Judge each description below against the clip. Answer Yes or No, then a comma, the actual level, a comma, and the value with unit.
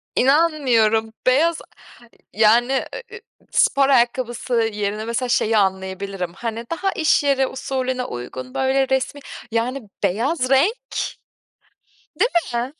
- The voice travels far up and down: No, average, 3.7 semitones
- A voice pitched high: Yes, very high, 250 Hz